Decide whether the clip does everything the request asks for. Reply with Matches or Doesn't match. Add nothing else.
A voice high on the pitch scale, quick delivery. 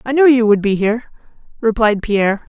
Doesn't match